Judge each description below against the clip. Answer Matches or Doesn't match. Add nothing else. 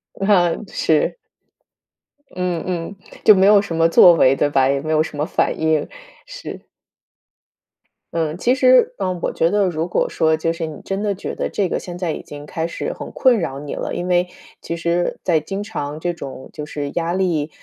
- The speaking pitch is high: Doesn't match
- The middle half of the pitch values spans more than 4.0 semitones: Doesn't match